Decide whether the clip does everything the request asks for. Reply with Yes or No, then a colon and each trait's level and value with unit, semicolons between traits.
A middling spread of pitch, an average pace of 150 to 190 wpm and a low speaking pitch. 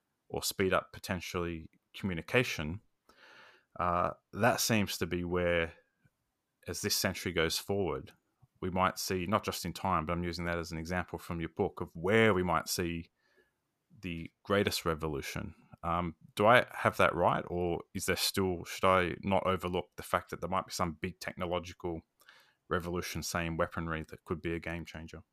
No: narrow, 2.0 semitones; average, 175 wpm; very low, 85 Hz